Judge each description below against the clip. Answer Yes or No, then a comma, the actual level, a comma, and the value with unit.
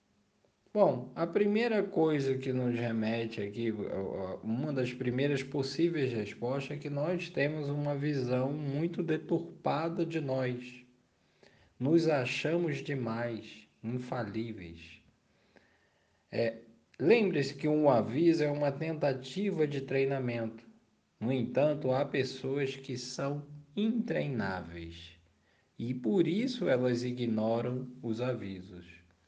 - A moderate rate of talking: No, slow, 105 wpm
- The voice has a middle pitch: No, low, 130 Hz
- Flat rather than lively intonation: No, average, 4.6 semitones